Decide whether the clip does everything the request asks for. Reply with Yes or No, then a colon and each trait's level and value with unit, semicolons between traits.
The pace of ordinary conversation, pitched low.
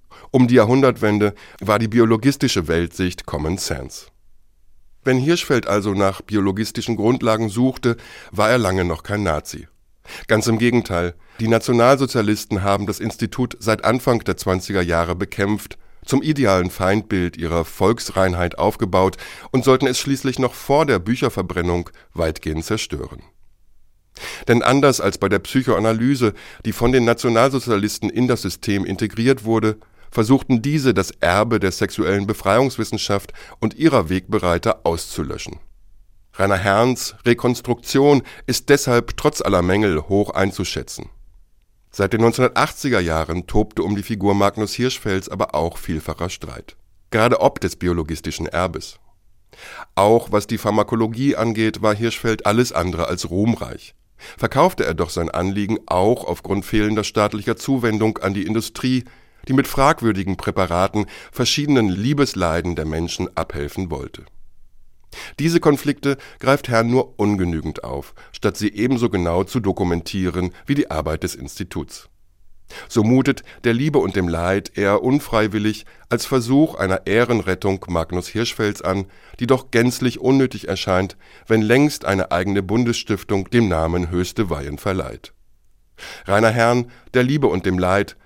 Yes: average, 135 wpm; low, 105 Hz